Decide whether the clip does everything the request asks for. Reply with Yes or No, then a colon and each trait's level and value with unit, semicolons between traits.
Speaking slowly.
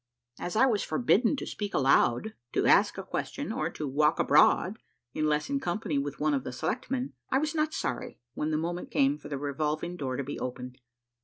No: fast, 205 wpm